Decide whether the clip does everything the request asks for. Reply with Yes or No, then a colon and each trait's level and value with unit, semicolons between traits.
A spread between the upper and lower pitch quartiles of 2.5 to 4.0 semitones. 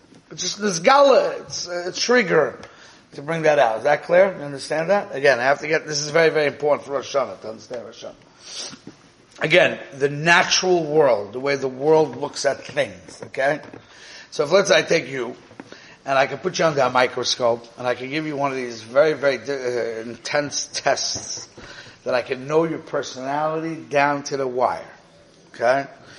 Yes: average, 3.2 semitones